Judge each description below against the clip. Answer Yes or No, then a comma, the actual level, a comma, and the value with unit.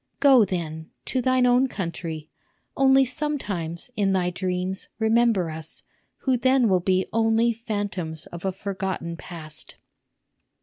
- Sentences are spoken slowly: Yes, slow, 130 wpm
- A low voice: No, high, 195 Hz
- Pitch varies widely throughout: Yes, wide, 5.8 semitones